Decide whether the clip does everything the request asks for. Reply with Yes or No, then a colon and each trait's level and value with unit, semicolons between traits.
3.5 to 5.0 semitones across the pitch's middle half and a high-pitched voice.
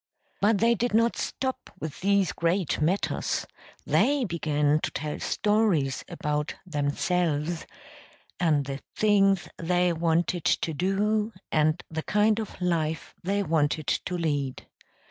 No: average, 4.7 semitones; medium, 175 Hz